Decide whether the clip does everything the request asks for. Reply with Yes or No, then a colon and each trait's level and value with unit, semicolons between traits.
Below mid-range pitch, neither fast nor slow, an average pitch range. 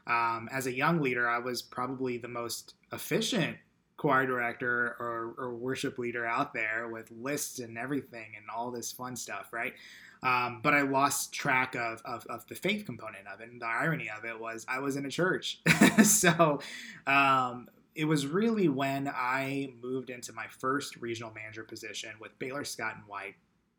Yes: low, 125 Hz; average, 180 wpm; average, 3.2 semitones